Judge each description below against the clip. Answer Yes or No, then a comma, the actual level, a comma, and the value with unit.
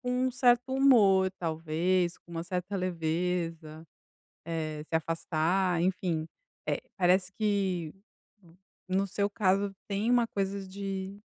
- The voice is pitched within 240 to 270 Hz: No, medium, 185 Hz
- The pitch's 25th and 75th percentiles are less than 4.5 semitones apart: Yes, average, 3.0 semitones